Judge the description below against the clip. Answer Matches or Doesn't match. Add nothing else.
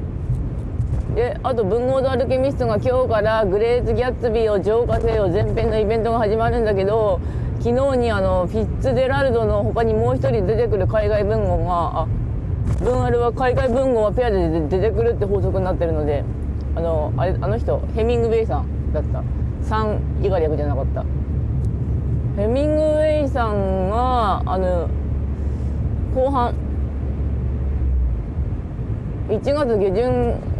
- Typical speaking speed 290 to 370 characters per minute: Matches